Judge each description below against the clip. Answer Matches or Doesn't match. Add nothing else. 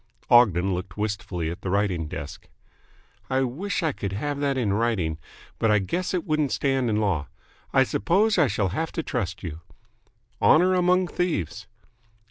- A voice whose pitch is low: Matches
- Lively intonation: Matches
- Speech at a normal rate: Matches